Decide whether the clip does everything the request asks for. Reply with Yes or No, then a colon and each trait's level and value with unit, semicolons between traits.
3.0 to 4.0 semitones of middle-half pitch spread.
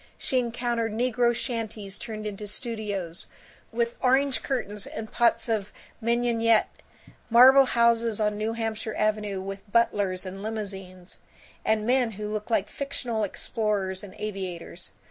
No: narrow, 2.5 semitones